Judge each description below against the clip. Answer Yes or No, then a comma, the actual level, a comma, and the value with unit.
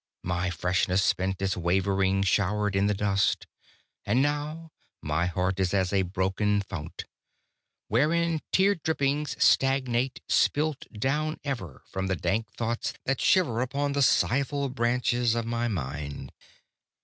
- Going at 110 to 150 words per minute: Yes, slow, 135 wpm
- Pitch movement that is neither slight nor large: No, wide, 6.4 semitones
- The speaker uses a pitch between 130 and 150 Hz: No, low, 110 Hz